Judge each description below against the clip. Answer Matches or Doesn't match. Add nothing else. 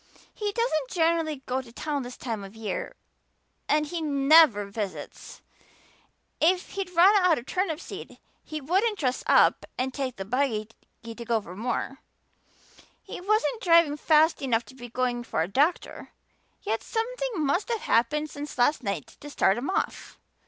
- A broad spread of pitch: Matches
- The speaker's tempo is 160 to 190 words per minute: Matches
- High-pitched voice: Matches